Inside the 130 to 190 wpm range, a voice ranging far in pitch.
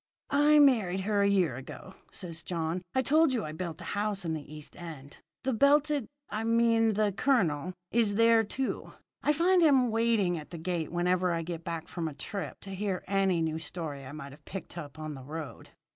No: fast, 205 wpm; wide, 5.9 semitones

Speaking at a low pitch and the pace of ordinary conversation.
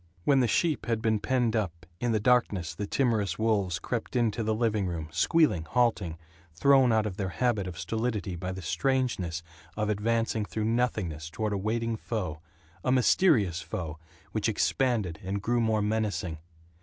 Yes: low, 110 Hz; average, 170 wpm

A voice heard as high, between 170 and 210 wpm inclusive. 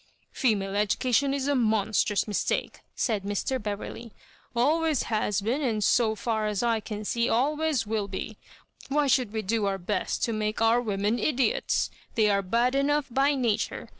Yes: high, 225 Hz; average, 180 wpm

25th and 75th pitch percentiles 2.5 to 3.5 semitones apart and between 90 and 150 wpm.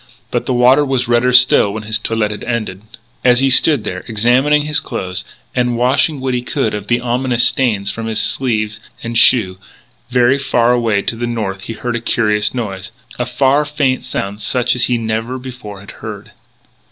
No: average, 2.9 semitones; average, 185 wpm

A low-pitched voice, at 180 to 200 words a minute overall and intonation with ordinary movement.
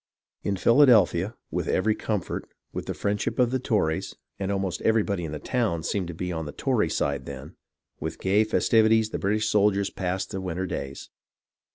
Yes: low, 100 Hz; average, 185 wpm; average, 3.9 semitones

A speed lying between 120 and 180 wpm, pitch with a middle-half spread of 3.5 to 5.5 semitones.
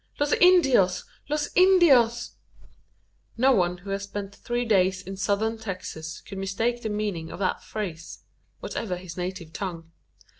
Yes: average, 145 wpm; average, 4.6 semitones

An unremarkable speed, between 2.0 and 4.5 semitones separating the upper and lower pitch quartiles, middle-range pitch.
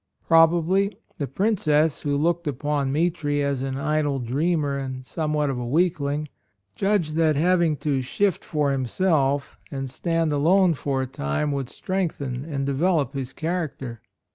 Yes: average, 150 wpm; average, 3.4 semitones; medium, 150 Hz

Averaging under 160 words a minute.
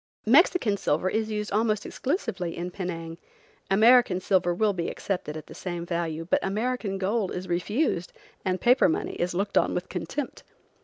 No: average, 165 wpm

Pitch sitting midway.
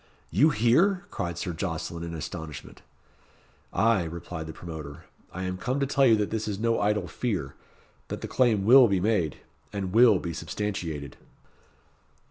No: very low, 95 Hz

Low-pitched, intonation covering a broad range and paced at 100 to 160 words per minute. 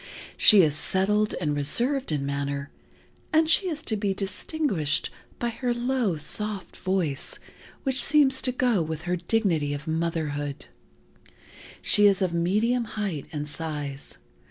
No: high, 190 Hz; wide, 7.8 semitones; average, 140 wpm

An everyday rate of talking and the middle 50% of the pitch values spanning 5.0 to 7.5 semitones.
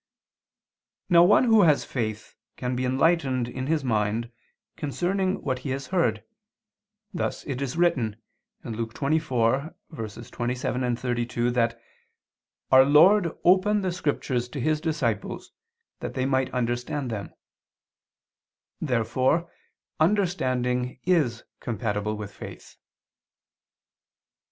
No: slow, 105 wpm; average, 5.3 semitones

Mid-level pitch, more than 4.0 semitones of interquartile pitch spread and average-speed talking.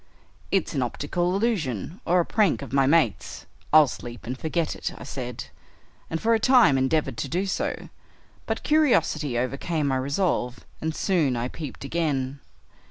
Yes: medium, 150 Hz; average, 5.2 semitones; average, 165 wpm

